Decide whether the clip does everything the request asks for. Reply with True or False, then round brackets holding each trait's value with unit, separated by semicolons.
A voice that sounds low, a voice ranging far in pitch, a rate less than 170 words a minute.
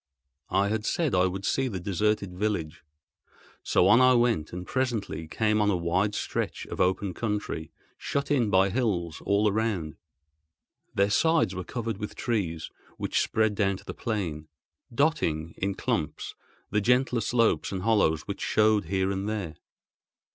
False (100 Hz; 3.8 semitones; 160 wpm)